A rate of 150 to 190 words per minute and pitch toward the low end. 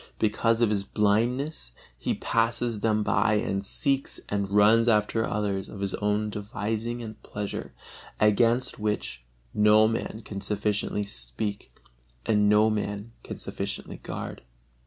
No: slow, 135 wpm; low, 105 Hz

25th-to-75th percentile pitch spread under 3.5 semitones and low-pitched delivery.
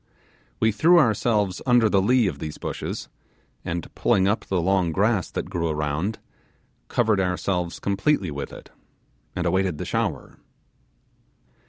No: average, 4.3 semitones; very low, 95 Hz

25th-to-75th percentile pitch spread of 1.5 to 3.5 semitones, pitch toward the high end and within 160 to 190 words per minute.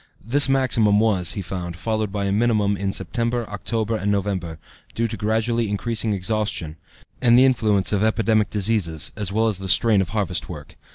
No: average, 2.7 semitones; low, 105 Hz; average, 180 wpm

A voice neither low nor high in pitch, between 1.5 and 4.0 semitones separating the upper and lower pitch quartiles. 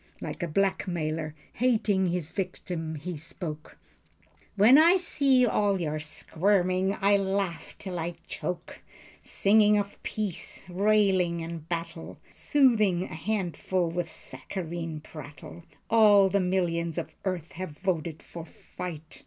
Yes: medium, 180 Hz; average, 3.4 semitones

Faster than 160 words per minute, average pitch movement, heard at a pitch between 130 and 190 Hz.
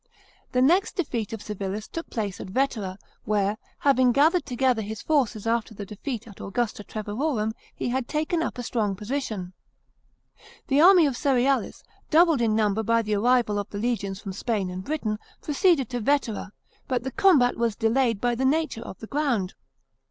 No: average, 175 wpm; average, 4.6 semitones; high, 235 Hz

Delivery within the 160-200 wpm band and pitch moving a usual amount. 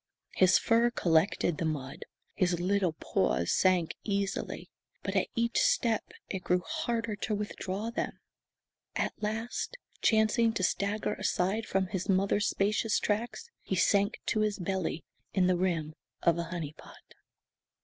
No: average, 145 wpm; average, 3.5 semitones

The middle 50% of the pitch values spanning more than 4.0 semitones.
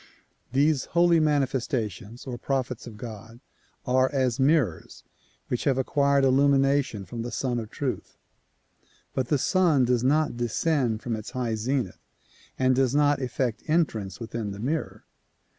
No: average, 3.3 semitones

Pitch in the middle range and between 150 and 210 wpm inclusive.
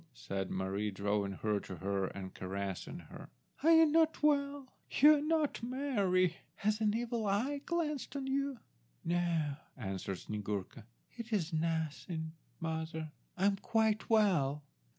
No: medium, 180 Hz; average, 140 wpm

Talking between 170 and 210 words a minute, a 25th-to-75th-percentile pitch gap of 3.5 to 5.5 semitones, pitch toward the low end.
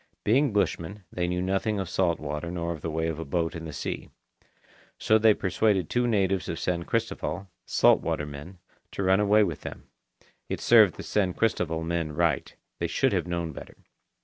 Yes: average, 195 wpm; average, 3.8 semitones; very low, 90 Hz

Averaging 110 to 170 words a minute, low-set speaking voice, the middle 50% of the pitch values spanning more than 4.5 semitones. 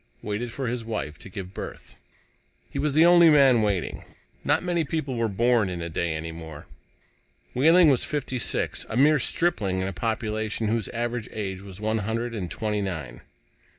No: average, 180 wpm; low, 110 Hz; average, 5.2 semitones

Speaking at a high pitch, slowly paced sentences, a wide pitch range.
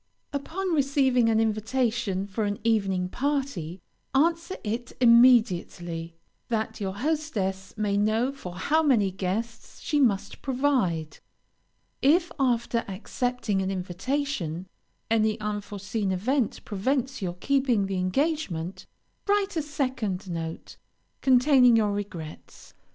Yes: high, 225 Hz; slow, 110 wpm; wide, 5.8 semitones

